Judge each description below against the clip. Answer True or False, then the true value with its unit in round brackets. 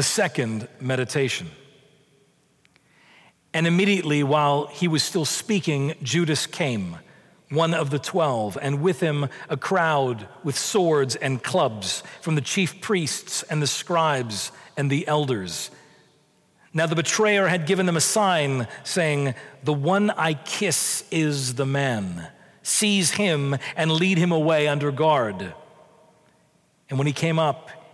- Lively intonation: False (3.3 semitones)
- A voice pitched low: False (155 Hz)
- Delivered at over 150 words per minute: False (135 wpm)